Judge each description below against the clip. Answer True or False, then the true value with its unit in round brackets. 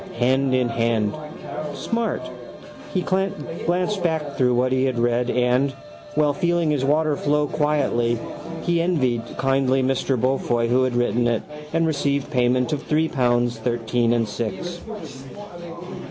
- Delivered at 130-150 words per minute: True (140 wpm)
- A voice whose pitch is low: True (130 Hz)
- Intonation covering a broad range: False (3.9 semitones)